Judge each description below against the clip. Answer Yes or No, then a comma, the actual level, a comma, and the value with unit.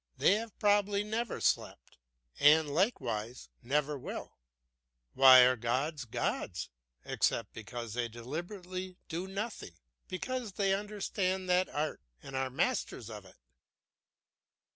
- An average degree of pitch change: No, wide, 7.9 semitones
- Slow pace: Yes, slow, 120 wpm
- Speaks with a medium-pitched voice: Yes, medium, 155 Hz